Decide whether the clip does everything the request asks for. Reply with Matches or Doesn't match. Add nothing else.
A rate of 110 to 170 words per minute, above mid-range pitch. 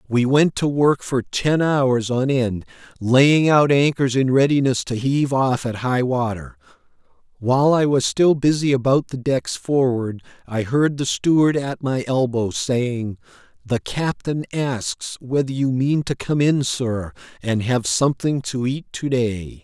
Doesn't match